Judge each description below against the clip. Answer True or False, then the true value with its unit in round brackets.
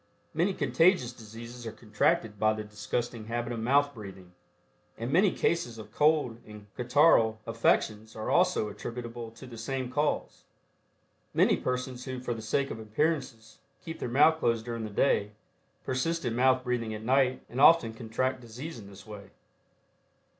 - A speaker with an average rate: True (160 wpm)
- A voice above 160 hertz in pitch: False (120 Hz)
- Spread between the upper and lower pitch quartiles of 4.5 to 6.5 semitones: False (3.2 semitones)